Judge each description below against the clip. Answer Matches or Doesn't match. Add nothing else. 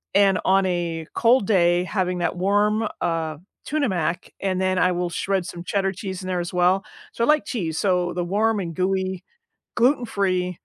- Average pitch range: Doesn't match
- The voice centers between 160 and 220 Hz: Matches